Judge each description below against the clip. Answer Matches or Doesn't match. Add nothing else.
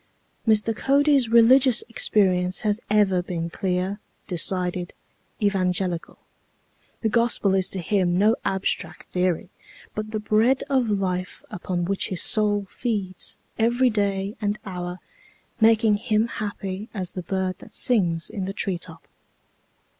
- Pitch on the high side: Matches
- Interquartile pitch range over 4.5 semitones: Doesn't match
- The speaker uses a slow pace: Matches